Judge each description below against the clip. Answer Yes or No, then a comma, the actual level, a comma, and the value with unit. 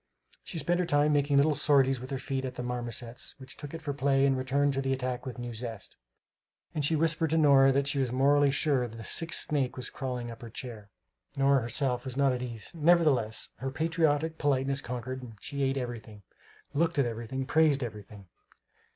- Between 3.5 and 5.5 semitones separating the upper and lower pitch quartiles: No, average, 2.8 semitones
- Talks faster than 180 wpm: Yes, average, 200 wpm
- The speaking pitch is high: No, low, 135 Hz